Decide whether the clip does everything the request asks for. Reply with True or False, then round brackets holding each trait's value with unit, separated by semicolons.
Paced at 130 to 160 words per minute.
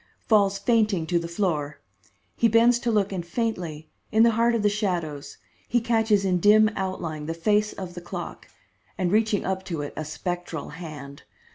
False (180 wpm)